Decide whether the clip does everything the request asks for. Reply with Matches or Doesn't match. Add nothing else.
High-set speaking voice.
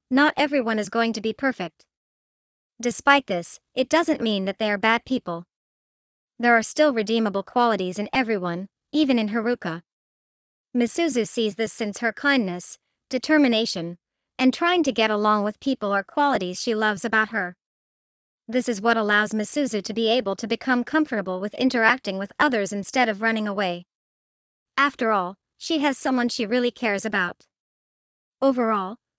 Matches